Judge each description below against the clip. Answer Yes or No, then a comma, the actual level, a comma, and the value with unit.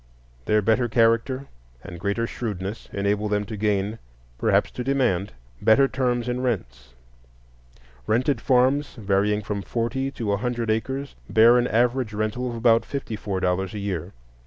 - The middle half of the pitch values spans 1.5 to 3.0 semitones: No, average, 3.4 semitones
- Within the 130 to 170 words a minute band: Yes, average, 155 wpm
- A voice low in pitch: Yes, low, 110 Hz